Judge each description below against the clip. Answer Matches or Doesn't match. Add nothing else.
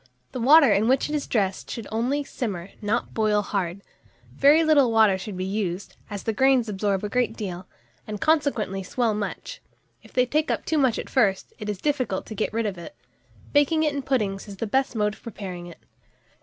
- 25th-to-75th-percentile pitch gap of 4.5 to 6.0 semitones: Matches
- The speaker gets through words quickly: Matches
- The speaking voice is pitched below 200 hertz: Doesn't match